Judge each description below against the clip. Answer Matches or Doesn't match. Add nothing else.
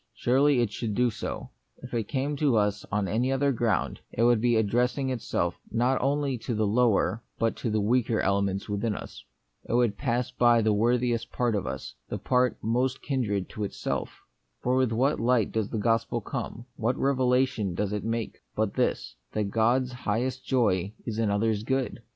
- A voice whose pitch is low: Matches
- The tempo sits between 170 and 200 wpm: Matches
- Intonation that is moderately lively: Matches